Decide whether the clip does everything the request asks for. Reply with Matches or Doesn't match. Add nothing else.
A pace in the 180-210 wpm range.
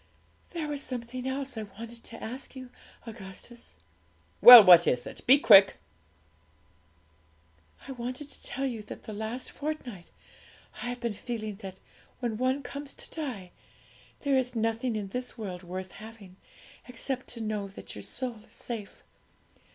Doesn't match